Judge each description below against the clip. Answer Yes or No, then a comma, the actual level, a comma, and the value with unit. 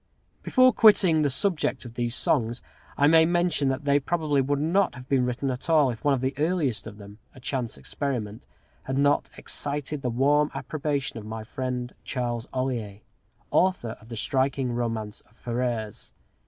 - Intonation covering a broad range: No, average, 3.8 semitones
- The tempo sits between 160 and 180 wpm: Yes, average, 175 wpm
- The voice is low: Yes, low, 130 Hz